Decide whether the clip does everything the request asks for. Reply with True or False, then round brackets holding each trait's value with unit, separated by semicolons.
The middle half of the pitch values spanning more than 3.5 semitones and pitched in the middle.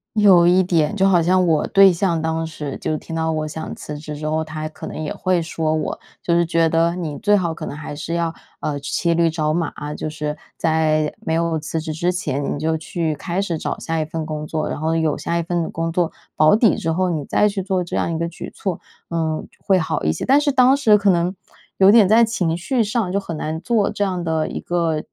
False (2.8 semitones; 165 Hz)